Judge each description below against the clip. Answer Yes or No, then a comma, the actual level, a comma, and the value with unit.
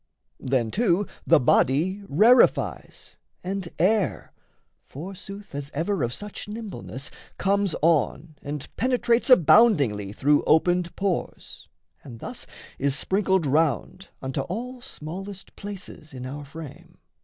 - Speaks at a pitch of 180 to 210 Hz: No, medium, 170 Hz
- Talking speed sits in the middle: No, slow, 115 wpm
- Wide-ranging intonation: Yes, wide, 6.2 semitones